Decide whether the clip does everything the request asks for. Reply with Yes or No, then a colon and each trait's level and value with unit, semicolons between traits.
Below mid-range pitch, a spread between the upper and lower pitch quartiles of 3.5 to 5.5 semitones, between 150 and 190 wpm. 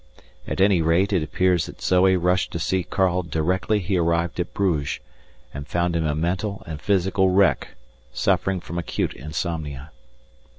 No: very low, 90 Hz; narrow, 2.5 semitones; average, 160 wpm